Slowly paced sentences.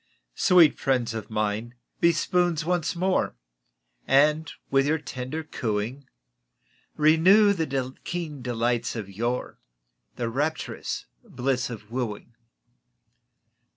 Yes: slow, 105 wpm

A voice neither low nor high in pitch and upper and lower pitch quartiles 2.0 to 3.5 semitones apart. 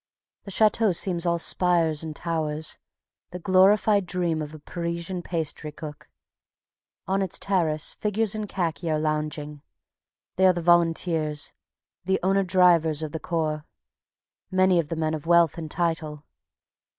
Yes: medium, 170 Hz; average, 3.0 semitones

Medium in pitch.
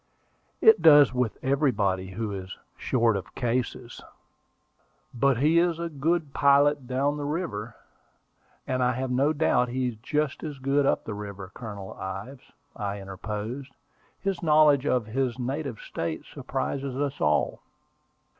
No: low, 130 Hz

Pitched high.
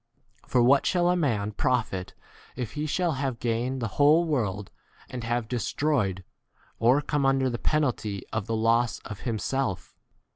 No: low, 125 Hz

